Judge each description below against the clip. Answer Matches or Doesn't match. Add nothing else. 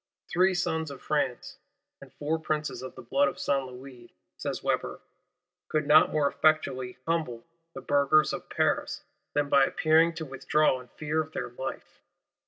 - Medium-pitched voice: Matches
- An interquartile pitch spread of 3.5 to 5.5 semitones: Doesn't match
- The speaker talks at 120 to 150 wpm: Doesn't match